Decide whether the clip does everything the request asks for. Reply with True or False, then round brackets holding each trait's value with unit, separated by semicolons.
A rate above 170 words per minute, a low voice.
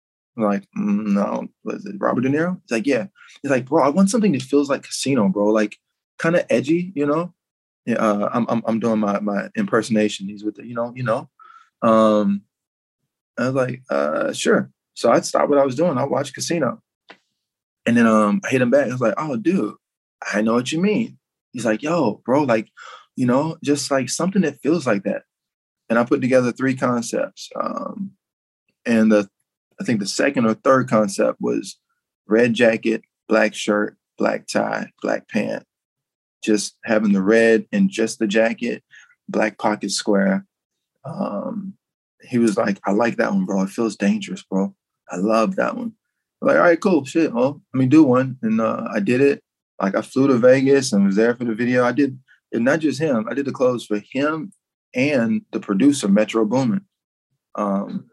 True (195 wpm; 120 Hz)